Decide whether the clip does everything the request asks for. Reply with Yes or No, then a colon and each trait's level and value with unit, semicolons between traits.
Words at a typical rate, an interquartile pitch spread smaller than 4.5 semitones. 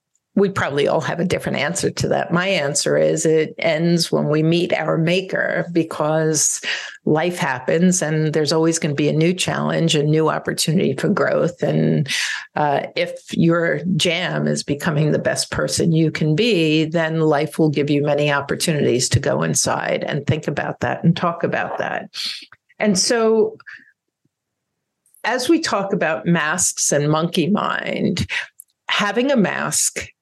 Yes: average, 160 wpm; narrow, 2.6 semitones